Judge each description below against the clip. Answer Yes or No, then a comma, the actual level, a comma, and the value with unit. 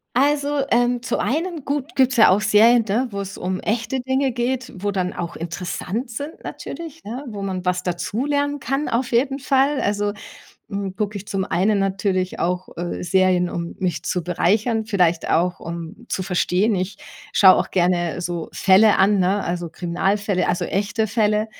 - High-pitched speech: Yes, high, 205 Hz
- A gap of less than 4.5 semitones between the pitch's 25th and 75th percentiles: No, average, 5.1 semitones